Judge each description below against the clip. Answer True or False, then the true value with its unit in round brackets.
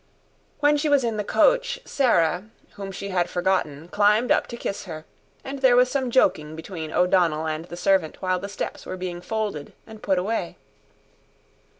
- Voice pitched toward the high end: True (195 Hz)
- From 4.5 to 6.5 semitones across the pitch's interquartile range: True (5.3 semitones)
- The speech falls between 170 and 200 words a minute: True (180 wpm)